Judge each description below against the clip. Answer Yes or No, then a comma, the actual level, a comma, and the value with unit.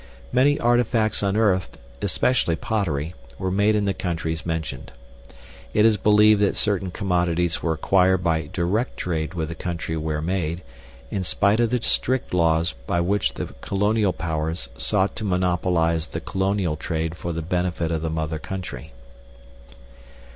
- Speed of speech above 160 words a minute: No, average, 150 wpm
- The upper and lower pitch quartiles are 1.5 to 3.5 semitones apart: No, average, 3.9 semitones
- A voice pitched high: No, very low, 90 Hz